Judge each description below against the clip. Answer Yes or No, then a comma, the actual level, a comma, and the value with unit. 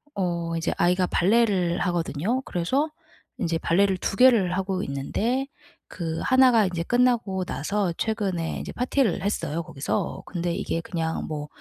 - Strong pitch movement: No, average, 4.7 semitones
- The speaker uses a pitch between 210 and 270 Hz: No, medium, 185 Hz